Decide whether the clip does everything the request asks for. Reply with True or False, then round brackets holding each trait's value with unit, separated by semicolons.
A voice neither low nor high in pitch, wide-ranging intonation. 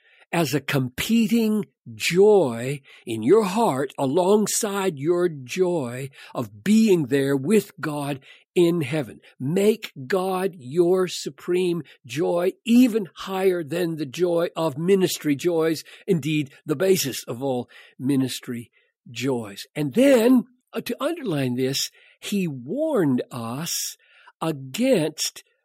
True (170 Hz; 6.8 semitones)